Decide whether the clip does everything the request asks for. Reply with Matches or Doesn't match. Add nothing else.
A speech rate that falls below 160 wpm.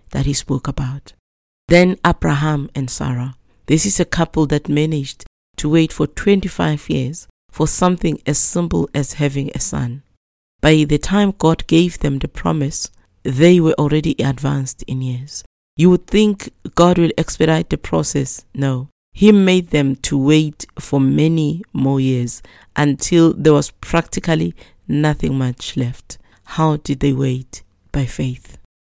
Matches